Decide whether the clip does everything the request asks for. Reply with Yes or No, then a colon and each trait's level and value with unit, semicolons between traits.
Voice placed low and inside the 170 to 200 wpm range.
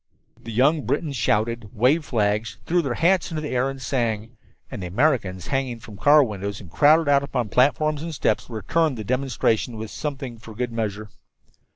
Yes: low, 125 Hz; average, 195 wpm